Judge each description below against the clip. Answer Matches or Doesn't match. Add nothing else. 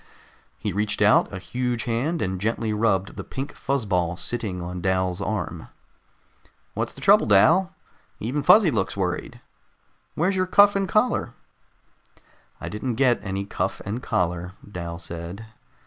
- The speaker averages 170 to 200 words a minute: Doesn't match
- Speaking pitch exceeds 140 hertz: Doesn't match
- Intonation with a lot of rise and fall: Matches